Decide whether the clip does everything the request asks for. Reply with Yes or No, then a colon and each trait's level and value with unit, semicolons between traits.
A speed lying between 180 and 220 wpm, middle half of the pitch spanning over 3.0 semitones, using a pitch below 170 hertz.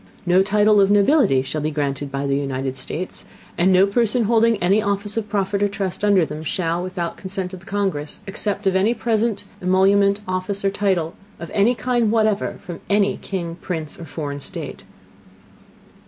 No: average, 185 wpm; average, 3.5 semitones; high, 195 Hz